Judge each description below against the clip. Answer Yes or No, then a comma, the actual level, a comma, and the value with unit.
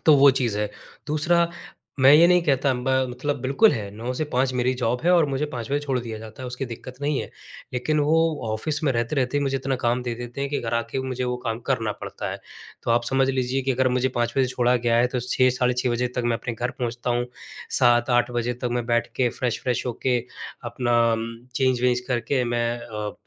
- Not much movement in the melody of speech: Yes, narrow, 2.1 semitones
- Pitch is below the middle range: Yes, low, 125 Hz